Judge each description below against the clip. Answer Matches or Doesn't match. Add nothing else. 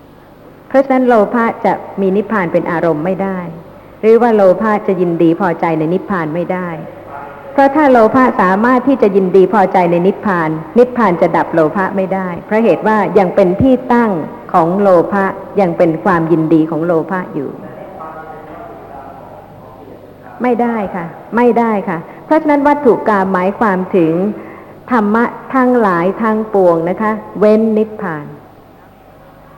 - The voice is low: Doesn't match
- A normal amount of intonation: Matches